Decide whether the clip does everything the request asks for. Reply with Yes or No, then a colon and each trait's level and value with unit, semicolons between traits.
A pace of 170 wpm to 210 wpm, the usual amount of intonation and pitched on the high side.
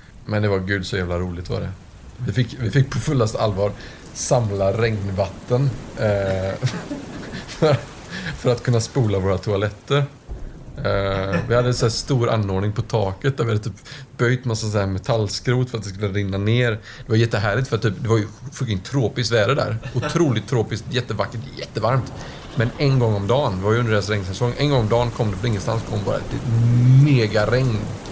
No: average, 190 wpm; average, 3.6 semitones; low, 115 Hz